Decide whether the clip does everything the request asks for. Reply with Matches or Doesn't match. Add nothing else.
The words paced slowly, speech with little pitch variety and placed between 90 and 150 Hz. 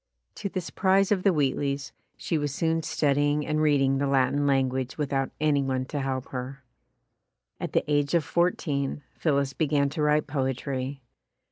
Doesn't match